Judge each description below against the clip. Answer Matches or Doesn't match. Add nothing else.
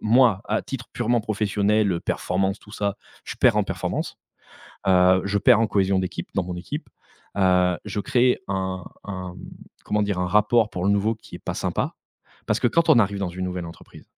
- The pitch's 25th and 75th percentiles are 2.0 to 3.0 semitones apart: Matches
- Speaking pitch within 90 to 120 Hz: Matches